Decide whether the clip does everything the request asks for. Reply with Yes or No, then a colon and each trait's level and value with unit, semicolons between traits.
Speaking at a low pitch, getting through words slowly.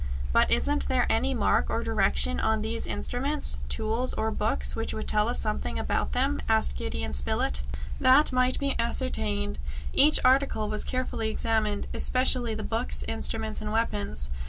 No: very low, 75 Hz; average, 155 wpm